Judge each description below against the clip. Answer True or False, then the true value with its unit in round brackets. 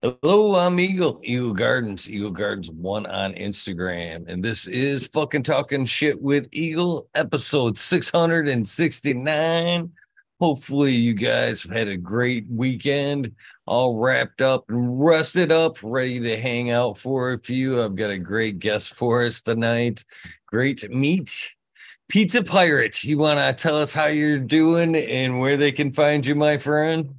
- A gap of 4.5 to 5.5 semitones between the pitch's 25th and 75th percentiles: True (4.9 semitones)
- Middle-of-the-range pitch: False (130 Hz)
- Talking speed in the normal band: True (165 wpm)